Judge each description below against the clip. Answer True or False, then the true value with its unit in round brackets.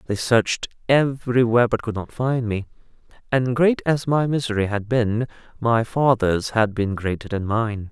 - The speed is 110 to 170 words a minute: True (165 wpm)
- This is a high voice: False (115 Hz)